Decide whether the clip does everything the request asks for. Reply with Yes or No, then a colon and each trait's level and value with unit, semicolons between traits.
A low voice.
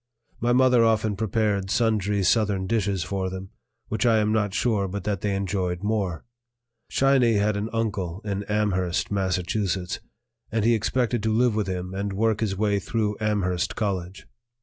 Yes: low, 105 Hz